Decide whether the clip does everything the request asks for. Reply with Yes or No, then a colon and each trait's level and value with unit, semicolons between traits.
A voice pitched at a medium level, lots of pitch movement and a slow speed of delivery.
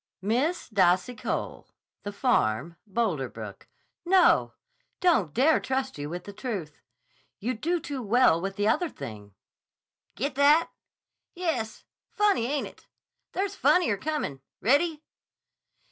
No: high, 240 Hz; wide, 8.2 semitones; slow, 125 wpm